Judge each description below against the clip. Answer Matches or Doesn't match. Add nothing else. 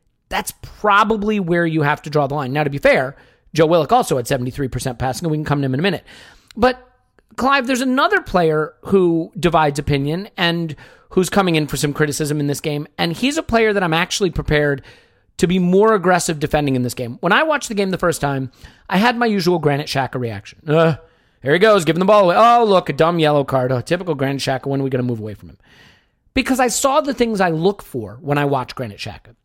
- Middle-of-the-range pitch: Matches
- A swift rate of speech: Matches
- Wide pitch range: Matches